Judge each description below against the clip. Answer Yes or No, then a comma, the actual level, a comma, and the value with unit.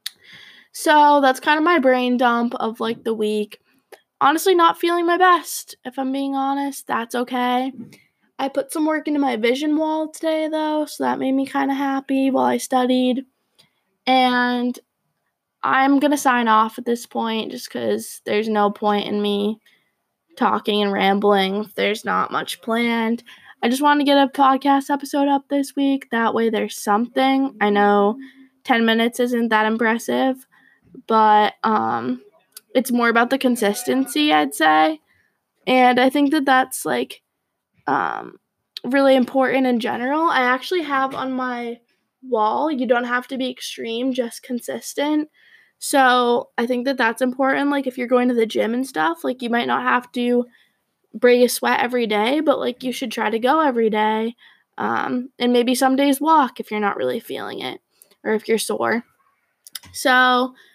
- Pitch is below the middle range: No, very high, 255 Hz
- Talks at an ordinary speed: Yes, average, 170 wpm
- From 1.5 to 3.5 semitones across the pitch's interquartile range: Yes, average, 3.2 semitones